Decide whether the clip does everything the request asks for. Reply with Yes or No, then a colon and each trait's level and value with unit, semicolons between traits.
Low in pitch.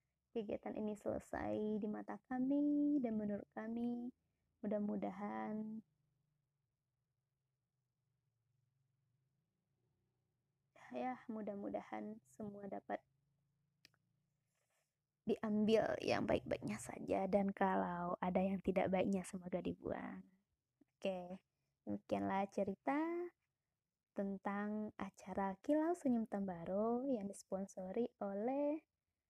No: high, 190 Hz